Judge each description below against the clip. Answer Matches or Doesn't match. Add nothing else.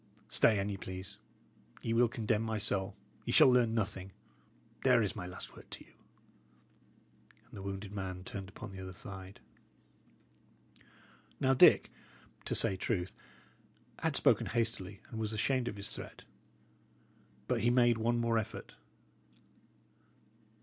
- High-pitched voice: Doesn't match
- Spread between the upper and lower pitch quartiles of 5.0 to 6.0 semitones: Doesn't match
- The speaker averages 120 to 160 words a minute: Matches